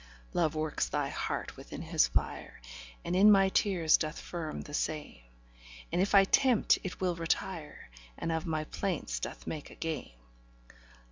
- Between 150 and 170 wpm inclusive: Yes, average, 160 wpm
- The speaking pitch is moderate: Yes, medium, 165 Hz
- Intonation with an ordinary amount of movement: Yes, average, 3.7 semitones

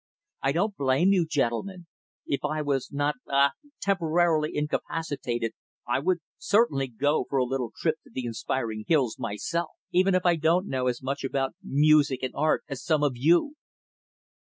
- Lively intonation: No, average, 4.2 semitones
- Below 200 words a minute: Yes, average, 165 wpm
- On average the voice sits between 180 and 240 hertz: No, medium, 145 Hz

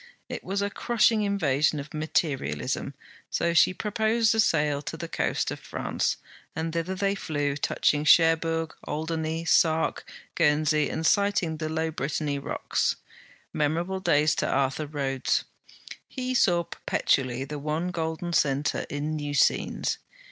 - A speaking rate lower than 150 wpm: Yes, average, 140 wpm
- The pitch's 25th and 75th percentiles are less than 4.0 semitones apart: Yes, average, 2.9 semitones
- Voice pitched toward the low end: No, medium, 160 Hz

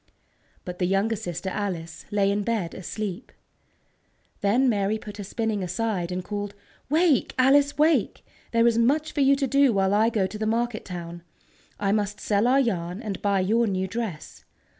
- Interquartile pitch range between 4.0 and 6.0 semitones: No, average, 3.6 semitones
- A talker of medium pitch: No, high, 210 Hz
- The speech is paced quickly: No, average, 180 wpm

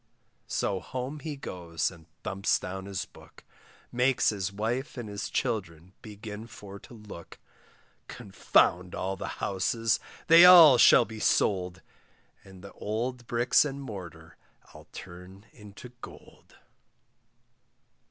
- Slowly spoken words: Yes, slow, 125 wpm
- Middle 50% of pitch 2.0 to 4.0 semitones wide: No, average, 4.5 semitones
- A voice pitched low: Yes, low, 105 Hz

